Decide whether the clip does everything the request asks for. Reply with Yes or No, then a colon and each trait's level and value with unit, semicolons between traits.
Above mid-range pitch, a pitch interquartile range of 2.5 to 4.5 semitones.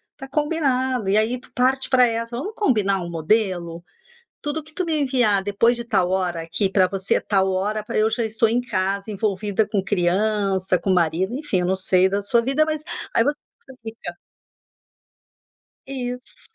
No: high, 215 Hz; average, 4.9 semitones